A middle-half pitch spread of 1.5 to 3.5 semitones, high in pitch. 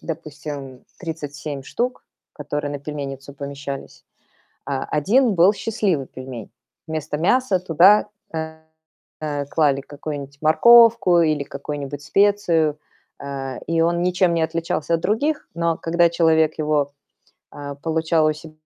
No: average, 3.0 semitones; medium, 155 Hz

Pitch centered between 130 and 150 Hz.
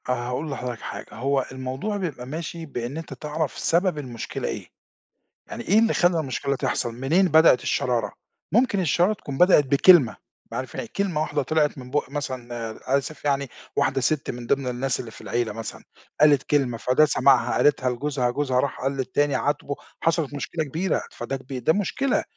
Yes: medium, 140 Hz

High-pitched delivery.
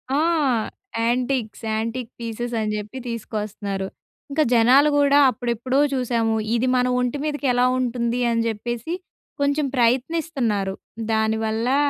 Yes: high, 240 Hz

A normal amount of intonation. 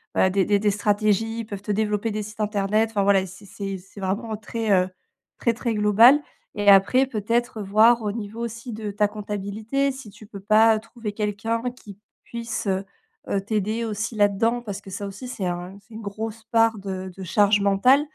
No: narrow, 2.1 semitones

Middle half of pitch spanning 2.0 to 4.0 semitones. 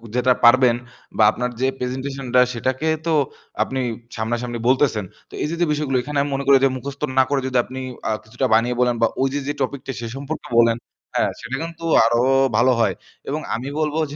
Yes: average, 2.8 semitones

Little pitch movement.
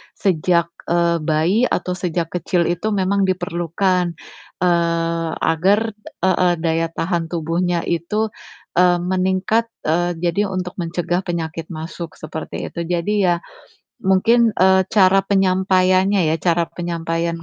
Yes: narrow, 2.0 semitones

